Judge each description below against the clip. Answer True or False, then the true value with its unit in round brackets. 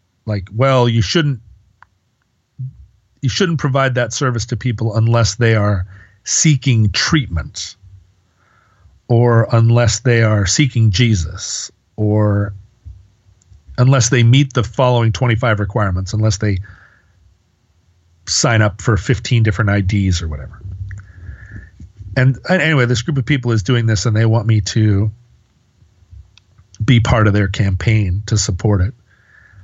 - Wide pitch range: False (3.8 semitones)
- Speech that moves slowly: True (125 wpm)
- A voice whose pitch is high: False (105 Hz)